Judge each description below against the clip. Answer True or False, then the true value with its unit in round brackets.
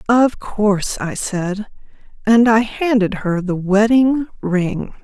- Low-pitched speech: False (210 Hz)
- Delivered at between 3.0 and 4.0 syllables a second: True (3.4 syllables/s)